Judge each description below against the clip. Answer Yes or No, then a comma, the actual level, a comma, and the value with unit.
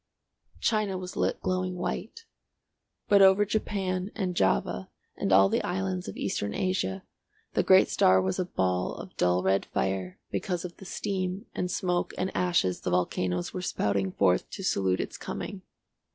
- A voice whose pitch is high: No, medium, 175 Hz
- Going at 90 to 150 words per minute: No, average, 165 wpm